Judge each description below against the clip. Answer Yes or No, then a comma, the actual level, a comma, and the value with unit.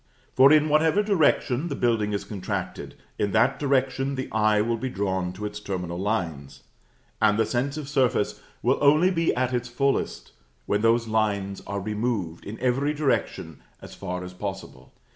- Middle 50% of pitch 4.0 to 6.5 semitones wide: Yes, average, 5.2 semitones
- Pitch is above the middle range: No, low, 115 Hz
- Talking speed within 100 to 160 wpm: No, average, 170 wpm